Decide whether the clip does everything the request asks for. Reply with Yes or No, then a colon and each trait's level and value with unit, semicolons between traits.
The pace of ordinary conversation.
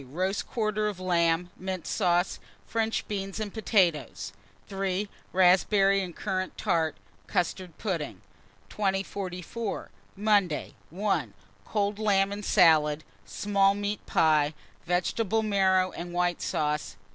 No: slow, 110 wpm